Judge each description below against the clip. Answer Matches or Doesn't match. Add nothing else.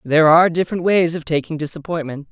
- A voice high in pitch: Doesn't match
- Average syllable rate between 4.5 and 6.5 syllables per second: Doesn't match